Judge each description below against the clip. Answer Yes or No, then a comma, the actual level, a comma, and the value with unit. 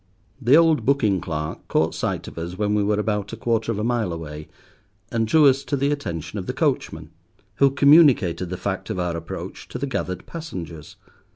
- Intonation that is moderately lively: No, wide, 7.9 semitones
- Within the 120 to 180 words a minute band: No, average, 200 wpm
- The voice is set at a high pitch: No, low, 105 Hz